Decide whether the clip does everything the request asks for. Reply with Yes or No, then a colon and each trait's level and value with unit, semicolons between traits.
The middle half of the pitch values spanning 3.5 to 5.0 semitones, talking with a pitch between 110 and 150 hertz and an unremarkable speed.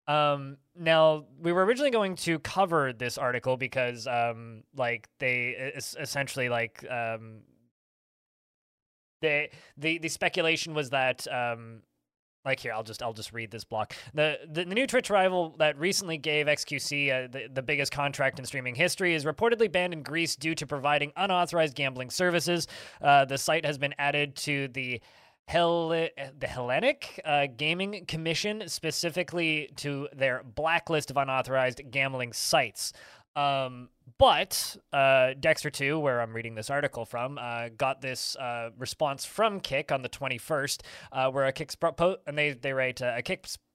Yes: average, 4.3 semitones; medium, 140 Hz; average, 165 wpm